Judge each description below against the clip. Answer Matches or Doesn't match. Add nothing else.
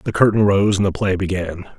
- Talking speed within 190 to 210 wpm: Doesn't match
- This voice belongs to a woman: Doesn't match